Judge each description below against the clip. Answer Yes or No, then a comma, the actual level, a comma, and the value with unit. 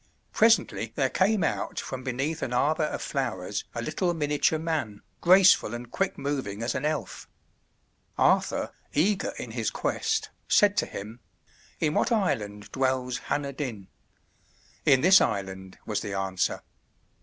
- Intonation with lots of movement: Yes, wide, 7.0 semitones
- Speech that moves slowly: No, average, 145 wpm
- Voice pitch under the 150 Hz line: Yes, low, 135 Hz